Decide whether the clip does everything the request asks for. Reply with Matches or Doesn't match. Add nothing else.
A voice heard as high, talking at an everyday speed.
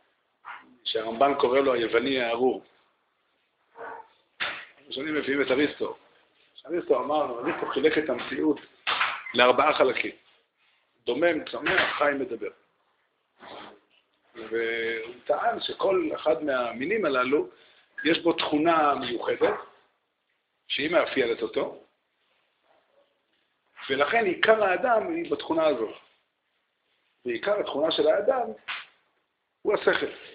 Doesn't match